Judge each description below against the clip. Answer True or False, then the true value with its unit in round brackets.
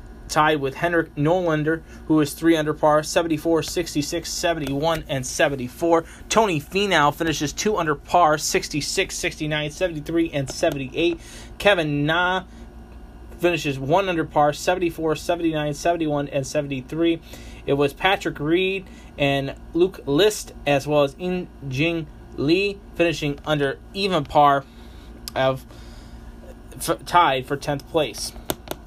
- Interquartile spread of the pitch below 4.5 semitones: True (3.3 semitones)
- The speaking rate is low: True (120 wpm)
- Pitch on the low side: False (155 Hz)